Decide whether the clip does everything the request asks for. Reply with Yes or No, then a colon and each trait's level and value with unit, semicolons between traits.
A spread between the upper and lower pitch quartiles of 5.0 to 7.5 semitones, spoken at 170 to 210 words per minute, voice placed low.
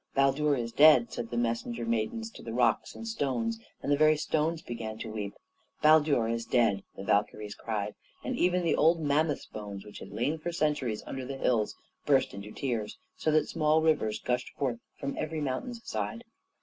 Yes: wide, 5.4 semitones; average, 190 wpm; low, 130 Hz